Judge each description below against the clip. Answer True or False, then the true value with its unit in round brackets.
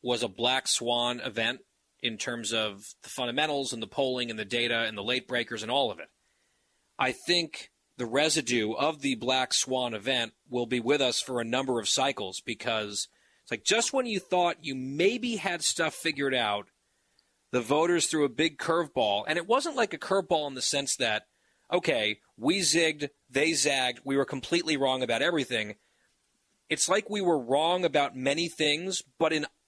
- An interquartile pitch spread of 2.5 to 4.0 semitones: False (5.3 semitones)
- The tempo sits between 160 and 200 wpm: True (185 wpm)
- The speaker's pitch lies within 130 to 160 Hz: True (135 Hz)